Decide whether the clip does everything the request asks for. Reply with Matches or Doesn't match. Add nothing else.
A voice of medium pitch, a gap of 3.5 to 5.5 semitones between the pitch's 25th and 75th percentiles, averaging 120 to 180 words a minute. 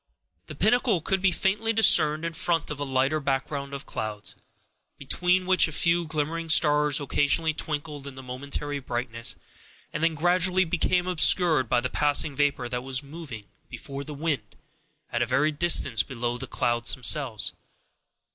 Matches